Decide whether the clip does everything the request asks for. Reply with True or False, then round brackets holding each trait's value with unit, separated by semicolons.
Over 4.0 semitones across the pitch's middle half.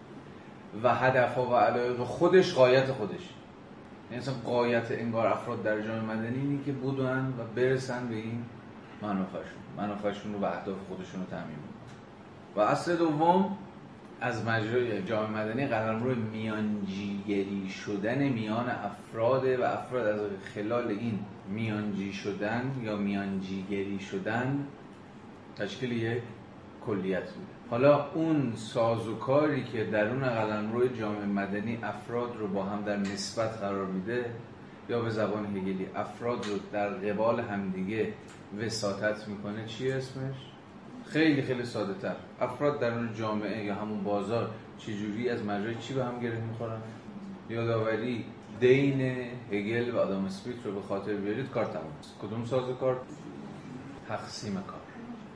False (3.2 semitones)